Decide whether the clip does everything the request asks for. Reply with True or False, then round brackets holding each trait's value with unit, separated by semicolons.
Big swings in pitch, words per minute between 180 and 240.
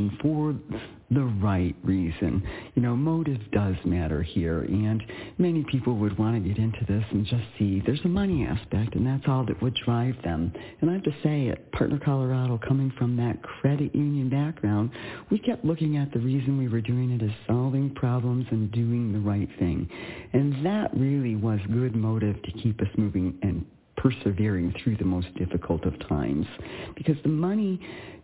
False (5.0 semitones; 185 wpm)